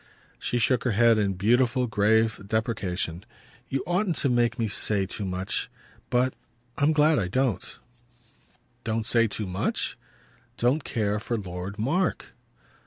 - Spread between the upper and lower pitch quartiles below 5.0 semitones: Yes, average, 3.8 semitones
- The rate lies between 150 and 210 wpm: No, average, 140 wpm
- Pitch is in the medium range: No, low, 115 Hz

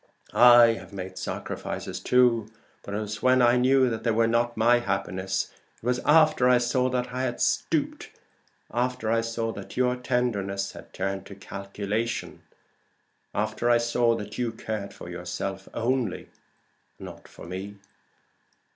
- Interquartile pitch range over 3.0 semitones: Yes, average, 3.6 semitones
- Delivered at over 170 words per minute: No, average, 155 wpm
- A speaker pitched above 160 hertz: No, low, 115 Hz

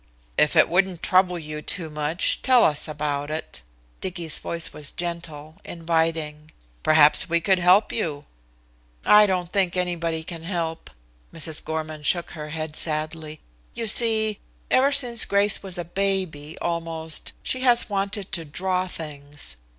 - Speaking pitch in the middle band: Yes, medium, 165 Hz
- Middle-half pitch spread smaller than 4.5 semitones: Yes, average, 3.4 semitones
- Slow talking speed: No, average, 145 wpm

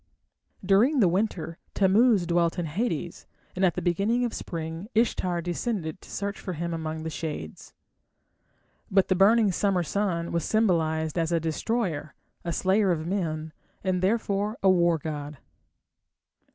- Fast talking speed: No, average, 150 wpm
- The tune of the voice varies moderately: Yes, average, 3.7 semitones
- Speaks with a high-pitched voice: No, medium, 180 Hz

